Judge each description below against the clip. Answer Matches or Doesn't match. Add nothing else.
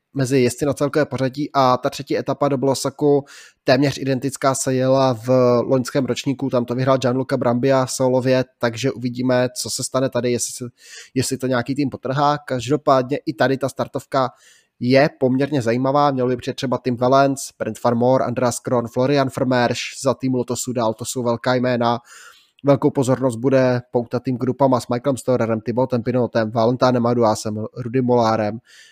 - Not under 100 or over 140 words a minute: Doesn't match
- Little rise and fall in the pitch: Matches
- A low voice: Matches